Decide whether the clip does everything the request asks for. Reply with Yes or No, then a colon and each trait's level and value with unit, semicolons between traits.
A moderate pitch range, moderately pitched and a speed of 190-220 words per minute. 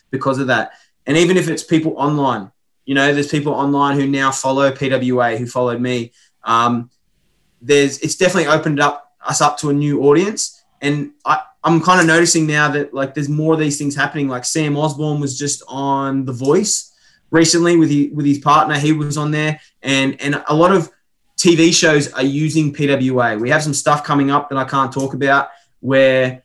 No: narrow, 2.1 semitones; medium, 145 Hz; average, 200 wpm